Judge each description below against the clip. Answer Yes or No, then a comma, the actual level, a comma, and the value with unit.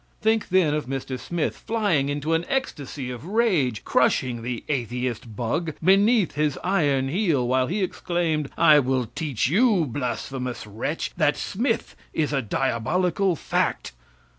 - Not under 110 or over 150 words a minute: Yes, average, 140 wpm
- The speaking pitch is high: No, medium, 150 Hz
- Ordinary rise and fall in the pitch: No, wide, 6.0 semitones